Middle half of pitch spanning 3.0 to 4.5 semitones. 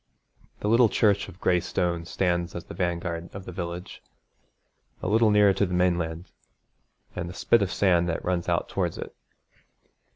No: narrow, 2.4 semitones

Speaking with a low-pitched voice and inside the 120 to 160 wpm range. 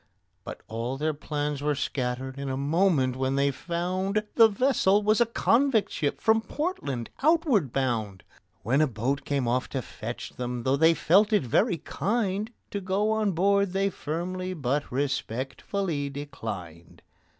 No: medium, 150 Hz; average, 155 wpm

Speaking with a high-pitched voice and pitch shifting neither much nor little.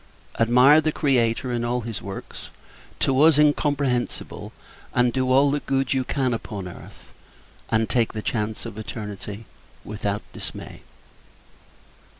No: low, 120 Hz; average, 3.6 semitones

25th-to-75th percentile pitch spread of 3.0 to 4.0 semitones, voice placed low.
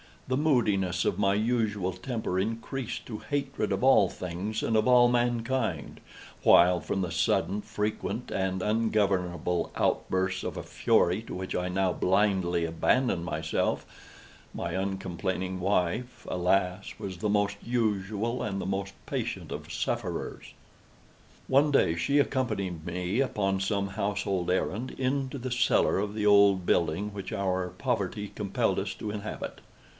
Yes: average, 3.7 semitones; low, 100 Hz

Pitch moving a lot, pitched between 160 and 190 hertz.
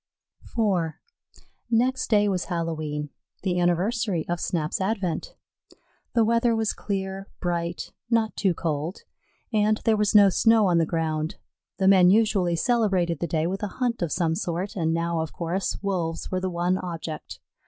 No: average, 3.8 semitones; medium, 185 Hz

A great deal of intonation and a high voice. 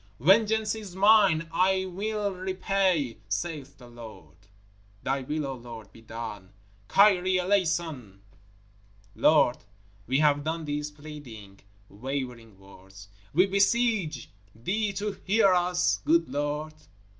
No: wide, 7.9 semitones; medium, 155 Hz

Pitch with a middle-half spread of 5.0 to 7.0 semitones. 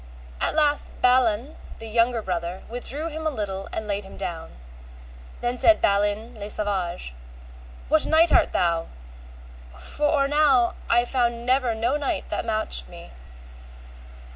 Yes: wide, 5.4 semitones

